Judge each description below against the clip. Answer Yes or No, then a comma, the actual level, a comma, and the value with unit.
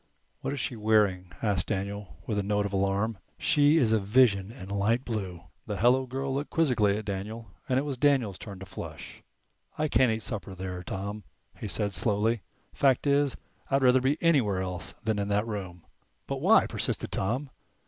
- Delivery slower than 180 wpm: No, average, 185 wpm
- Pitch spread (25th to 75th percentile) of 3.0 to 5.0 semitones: Yes, average, 4.6 semitones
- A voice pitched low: Yes, low, 110 Hz